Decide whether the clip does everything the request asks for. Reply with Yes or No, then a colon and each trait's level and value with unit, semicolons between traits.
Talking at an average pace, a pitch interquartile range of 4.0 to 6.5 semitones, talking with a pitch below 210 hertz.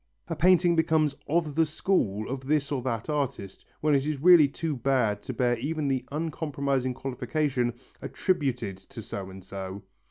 Yes: average, 165 wpm; average, 4.3 semitones; low, 135 Hz